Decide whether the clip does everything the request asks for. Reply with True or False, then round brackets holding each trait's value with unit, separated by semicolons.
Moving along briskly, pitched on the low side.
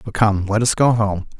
True (260 wpm; 105 Hz)